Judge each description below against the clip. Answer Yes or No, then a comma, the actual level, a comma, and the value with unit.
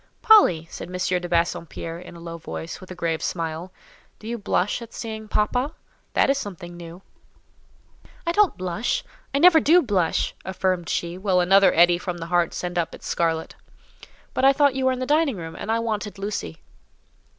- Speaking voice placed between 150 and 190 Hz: Yes, medium, 185 Hz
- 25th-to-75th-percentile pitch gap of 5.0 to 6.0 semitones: Yes, wide, 5.5 semitones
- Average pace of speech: Yes, average, 185 wpm